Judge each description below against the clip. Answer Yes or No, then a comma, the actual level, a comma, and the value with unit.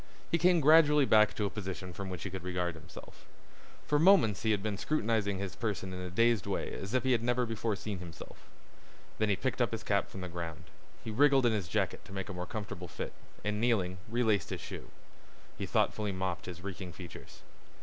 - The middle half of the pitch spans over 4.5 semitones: No, average, 4.1 semitones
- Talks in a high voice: No, low, 100 Hz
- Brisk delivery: Yes, fast, 215 wpm